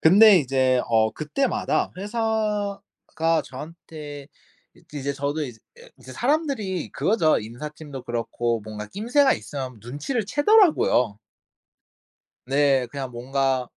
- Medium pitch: Yes, medium, 145 Hz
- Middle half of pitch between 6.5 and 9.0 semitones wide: Yes, wide, 8.2 semitones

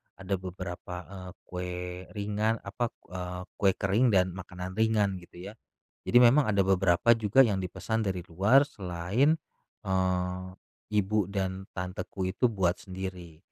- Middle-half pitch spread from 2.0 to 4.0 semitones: Yes, narrow, 2.6 semitones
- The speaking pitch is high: No, very low, 95 Hz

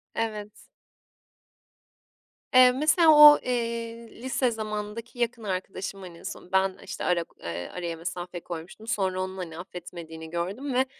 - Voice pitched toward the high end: Yes, high, 195 Hz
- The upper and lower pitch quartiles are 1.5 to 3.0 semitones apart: No, average, 4.9 semitones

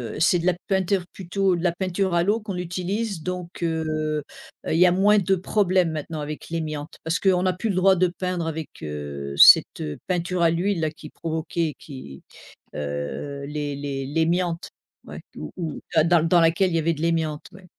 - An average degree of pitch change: Yes, average, 3.0 semitones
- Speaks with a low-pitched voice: No, medium, 170 Hz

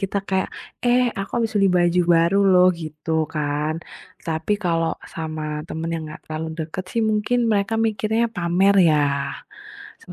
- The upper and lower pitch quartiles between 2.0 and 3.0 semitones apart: No, average, 4.0 semitones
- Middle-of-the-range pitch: Yes, medium, 175 Hz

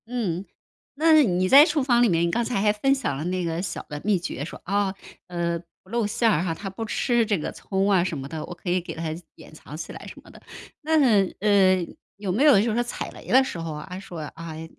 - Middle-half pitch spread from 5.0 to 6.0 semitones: Yes, average, 5.3 semitones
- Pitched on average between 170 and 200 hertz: Yes, high, 190 Hz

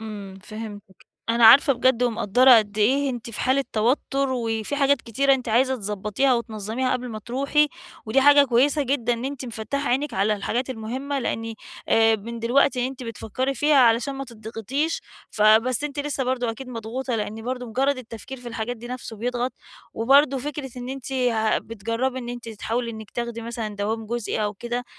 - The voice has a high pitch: Yes, high, 240 Hz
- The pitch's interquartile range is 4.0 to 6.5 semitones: No, average, 3.0 semitones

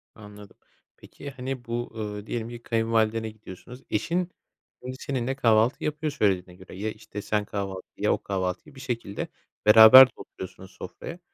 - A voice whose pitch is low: Yes, low, 110 Hz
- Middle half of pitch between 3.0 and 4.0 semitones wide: Yes, average, 3.7 semitones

